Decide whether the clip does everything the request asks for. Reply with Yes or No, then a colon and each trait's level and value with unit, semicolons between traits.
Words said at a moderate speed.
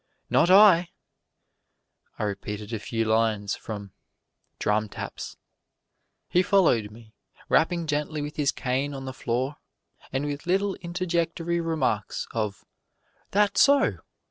No: slow, 120 wpm